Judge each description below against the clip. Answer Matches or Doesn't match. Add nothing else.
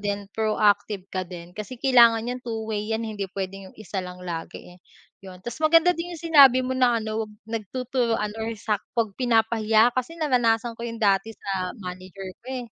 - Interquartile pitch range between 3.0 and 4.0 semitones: Matches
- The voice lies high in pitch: Matches